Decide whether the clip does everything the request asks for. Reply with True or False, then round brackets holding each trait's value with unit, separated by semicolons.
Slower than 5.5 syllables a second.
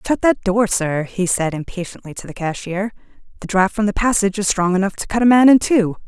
False (5.8 syllables/s)